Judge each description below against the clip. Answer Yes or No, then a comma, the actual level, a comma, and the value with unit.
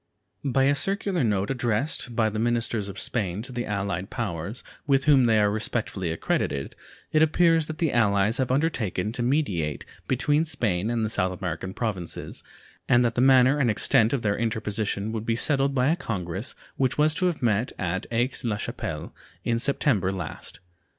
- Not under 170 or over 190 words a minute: Yes, average, 180 wpm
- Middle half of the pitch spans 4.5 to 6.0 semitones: Yes, average, 5.0 semitones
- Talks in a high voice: No, low, 115 Hz